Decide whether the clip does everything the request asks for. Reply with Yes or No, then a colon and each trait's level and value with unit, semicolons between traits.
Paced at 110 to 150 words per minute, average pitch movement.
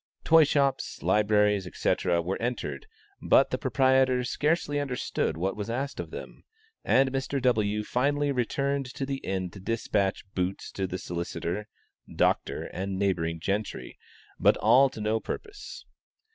No: average, 140 wpm; wide, 5.9 semitones